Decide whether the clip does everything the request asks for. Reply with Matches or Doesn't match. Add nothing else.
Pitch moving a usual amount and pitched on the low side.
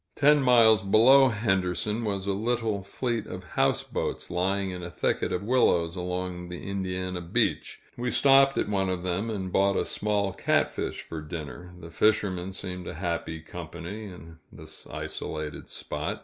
Matches